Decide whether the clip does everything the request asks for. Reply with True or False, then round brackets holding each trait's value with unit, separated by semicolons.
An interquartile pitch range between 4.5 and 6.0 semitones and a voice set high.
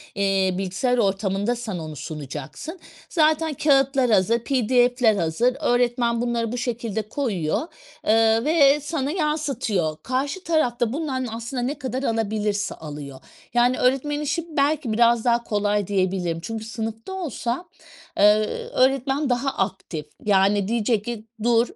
True (4.8 semitones; 235 Hz)